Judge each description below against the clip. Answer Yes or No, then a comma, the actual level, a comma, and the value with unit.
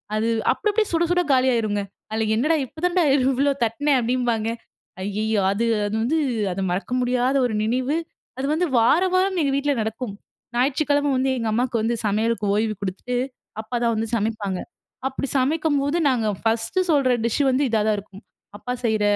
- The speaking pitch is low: No, high, 245 Hz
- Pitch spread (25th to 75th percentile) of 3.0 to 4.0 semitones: No, average, 4.4 semitones